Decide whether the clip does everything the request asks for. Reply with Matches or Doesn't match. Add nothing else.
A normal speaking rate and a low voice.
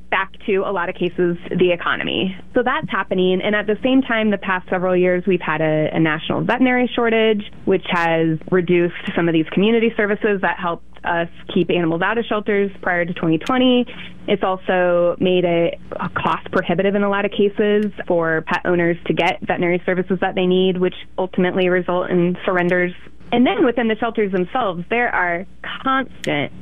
Doesn't match